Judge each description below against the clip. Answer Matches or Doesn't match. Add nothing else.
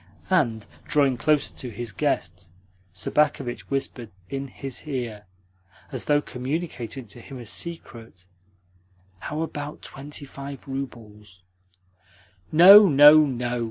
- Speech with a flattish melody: Doesn't match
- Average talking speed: Doesn't match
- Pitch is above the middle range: Doesn't match